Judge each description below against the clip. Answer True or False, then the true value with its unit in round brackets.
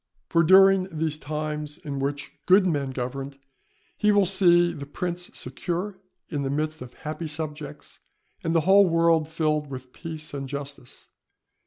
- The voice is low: False (155 Hz)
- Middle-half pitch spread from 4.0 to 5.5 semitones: False (3.3 semitones)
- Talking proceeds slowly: False (155 wpm)